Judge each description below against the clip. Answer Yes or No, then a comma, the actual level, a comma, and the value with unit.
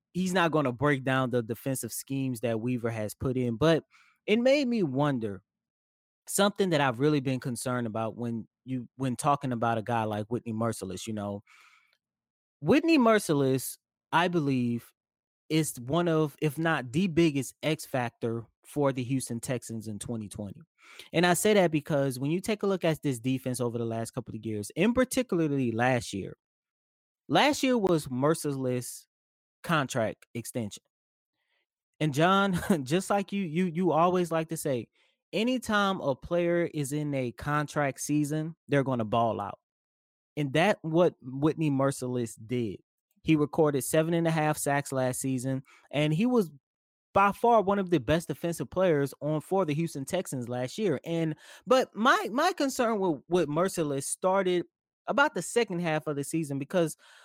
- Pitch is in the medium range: Yes, medium, 150 Hz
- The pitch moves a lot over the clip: Yes, wide, 5.8 semitones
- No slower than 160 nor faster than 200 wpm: Yes, average, 170 wpm